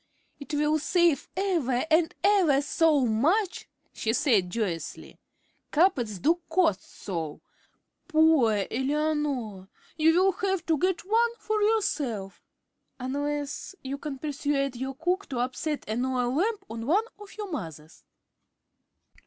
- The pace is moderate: No, slow, 130 wpm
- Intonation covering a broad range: Yes, wide, 6.1 semitones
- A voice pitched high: Yes, very high, 295 Hz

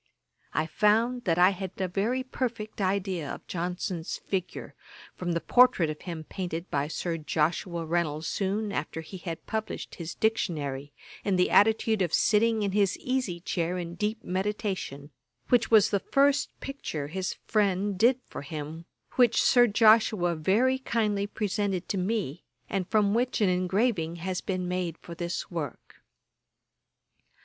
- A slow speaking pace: No, average, 155 wpm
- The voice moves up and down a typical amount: Yes, average, 4.2 semitones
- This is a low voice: No, high, 190 Hz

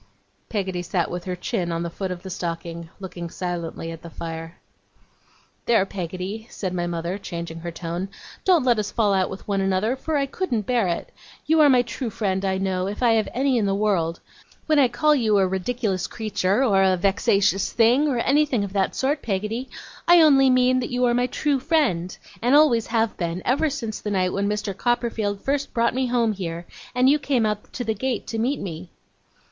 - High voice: Yes, high, 210 Hz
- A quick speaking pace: Yes, fast, 210 wpm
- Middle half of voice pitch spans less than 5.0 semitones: No, average, 5.3 semitones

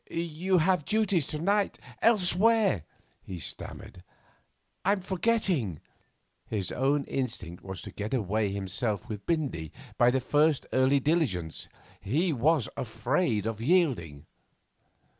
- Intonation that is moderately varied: No, wide, 8.9 semitones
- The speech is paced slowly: Yes, slow, 120 wpm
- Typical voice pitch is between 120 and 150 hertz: Yes, low, 135 Hz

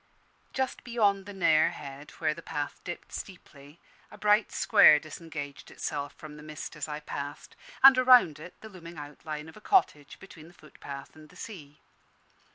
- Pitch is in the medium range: Yes, medium, 155 Hz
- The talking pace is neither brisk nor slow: Yes, average, 170 wpm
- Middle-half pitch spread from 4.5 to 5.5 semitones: Yes, average, 4.8 semitones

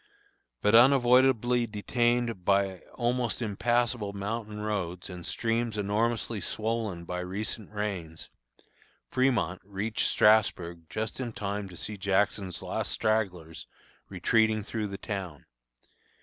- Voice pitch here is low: Yes, low, 105 Hz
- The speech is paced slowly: Yes, slow, 110 wpm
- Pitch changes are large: No, average, 3.1 semitones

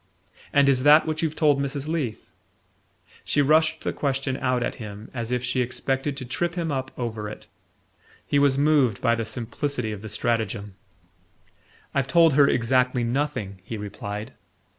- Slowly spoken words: No, average, 165 wpm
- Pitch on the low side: Yes, low, 130 Hz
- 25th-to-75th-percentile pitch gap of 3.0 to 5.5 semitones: Yes, average, 3.9 semitones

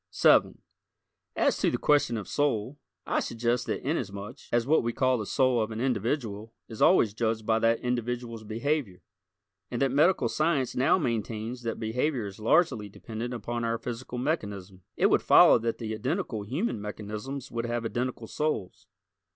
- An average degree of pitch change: Yes, average, 3.0 semitones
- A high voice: No, low, 120 Hz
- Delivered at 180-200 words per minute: No, average, 165 wpm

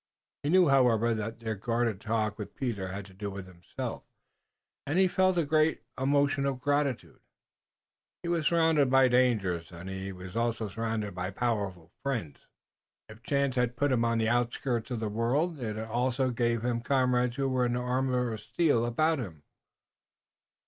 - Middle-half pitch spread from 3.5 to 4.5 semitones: Yes, average, 3.9 semitones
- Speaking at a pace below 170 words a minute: No, average, 175 wpm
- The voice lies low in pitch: Yes, low, 120 Hz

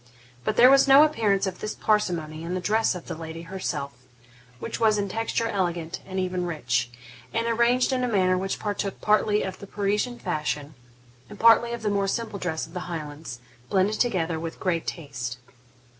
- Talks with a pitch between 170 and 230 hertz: Yes, high, 190 Hz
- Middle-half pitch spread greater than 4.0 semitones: Yes, average, 4.9 semitones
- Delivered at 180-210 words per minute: Yes, average, 190 wpm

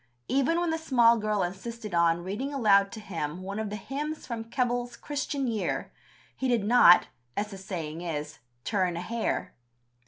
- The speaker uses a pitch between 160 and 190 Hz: No, high, 215 Hz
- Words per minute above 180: No, average, 175 wpm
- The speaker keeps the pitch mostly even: No, average, 4.9 semitones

